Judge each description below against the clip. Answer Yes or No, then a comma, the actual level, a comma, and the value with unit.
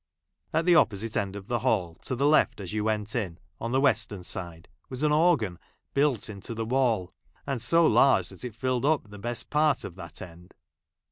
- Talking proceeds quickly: Yes, fast, 215 wpm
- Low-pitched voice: Yes, low, 115 Hz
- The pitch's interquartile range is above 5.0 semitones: Yes, wide, 5.4 semitones